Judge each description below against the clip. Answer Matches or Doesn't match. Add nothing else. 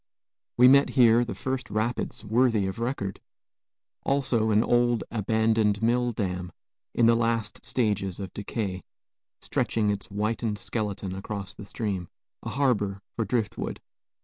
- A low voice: Matches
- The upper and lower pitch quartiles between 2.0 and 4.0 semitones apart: Matches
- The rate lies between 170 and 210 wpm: Doesn't match